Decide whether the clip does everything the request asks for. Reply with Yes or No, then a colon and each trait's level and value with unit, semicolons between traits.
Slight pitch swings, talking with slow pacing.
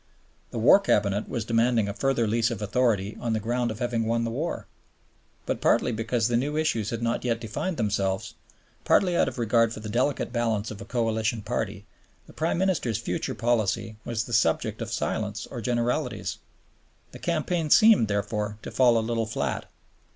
No: narrow, 2.2 semitones; average, 185 wpm